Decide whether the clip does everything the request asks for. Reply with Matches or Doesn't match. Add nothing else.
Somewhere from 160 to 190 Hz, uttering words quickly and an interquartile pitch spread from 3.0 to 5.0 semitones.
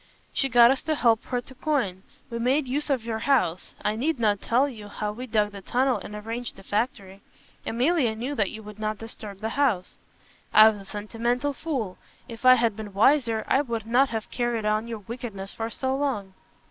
Doesn't match